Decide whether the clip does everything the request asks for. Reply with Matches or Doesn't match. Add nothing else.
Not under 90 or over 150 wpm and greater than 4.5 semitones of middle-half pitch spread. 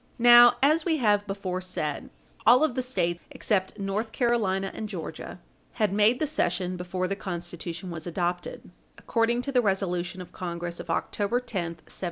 Doesn't match